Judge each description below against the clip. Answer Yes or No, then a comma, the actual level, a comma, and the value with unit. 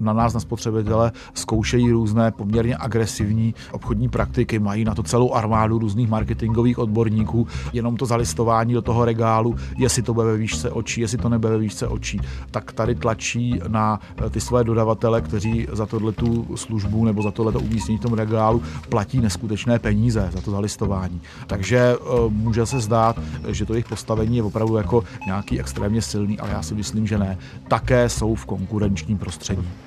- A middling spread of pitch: No, narrow, 1.8 semitones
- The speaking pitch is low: Yes, low, 110 Hz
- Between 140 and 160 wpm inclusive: No, fast, 170 wpm